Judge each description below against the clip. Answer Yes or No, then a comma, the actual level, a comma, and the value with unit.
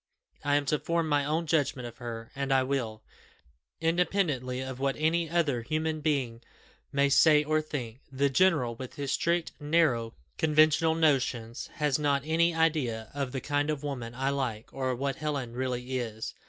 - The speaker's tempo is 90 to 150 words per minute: No, average, 175 wpm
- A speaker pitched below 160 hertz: Yes, medium, 140 Hz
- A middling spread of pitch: Yes, average, 3.6 semitones